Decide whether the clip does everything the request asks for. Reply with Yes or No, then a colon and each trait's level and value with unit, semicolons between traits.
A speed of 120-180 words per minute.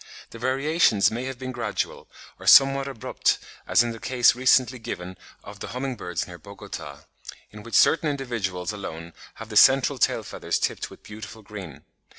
Yes: average, 170 wpm